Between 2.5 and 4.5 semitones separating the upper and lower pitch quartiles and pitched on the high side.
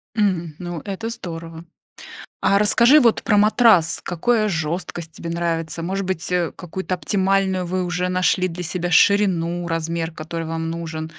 No: average, 2.9 semitones; medium, 175 Hz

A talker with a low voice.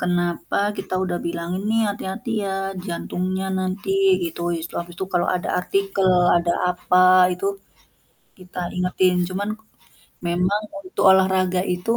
No: medium, 185 Hz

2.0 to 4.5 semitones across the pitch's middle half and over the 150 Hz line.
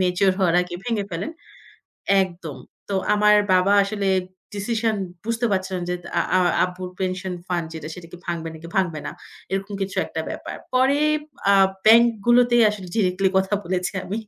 Yes: average, 2.8 semitones; high, 190 Hz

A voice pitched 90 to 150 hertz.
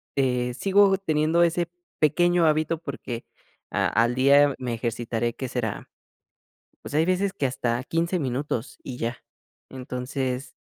Yes: low, 135 Hz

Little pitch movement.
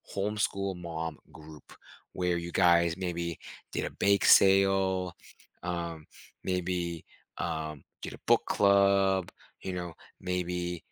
Yes: narrow, 2.1 semitones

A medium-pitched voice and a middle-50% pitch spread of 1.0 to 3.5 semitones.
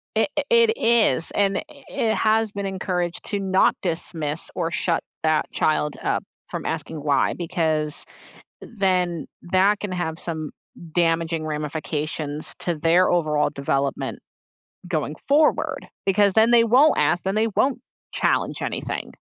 No: medium, 175 Hz; average, 4.5 semitones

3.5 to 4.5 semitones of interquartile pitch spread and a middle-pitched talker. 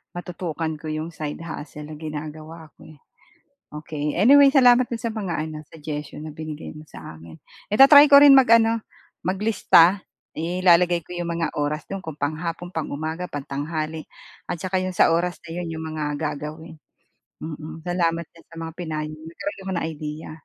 No: average, 2.8 semitones; medium, 160 Hz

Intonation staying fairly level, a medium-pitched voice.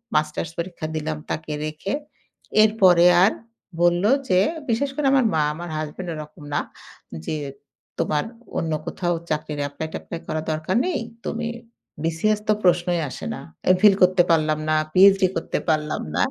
No: average, 3.4 semitones; medium, 170 Hz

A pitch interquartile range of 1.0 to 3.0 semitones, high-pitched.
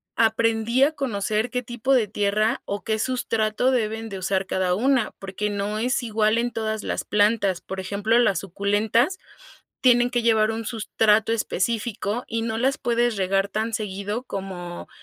Yes: average, 2.7 semitones; high, 220 Hz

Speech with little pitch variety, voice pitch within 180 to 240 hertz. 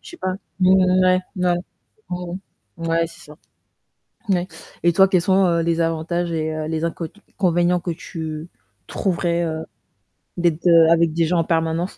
No: narrow, 1.5 semitones; medium, 170 Hz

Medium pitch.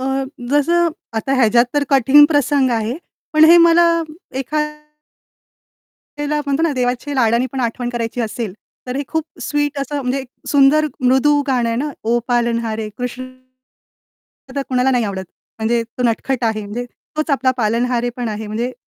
No: very high, 255 Hz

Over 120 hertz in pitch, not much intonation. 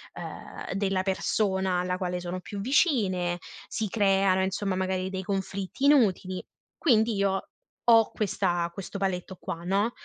Yes: high, 190 Hz; narrow, 2.0 semitones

